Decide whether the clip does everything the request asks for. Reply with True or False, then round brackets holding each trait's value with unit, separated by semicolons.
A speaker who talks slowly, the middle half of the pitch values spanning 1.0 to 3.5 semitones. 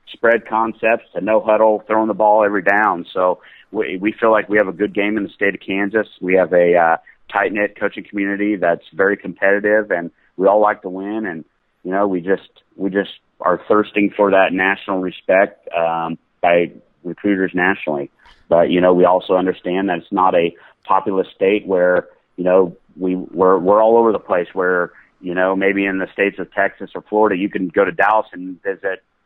False (205 wpm; 2.4 semitones)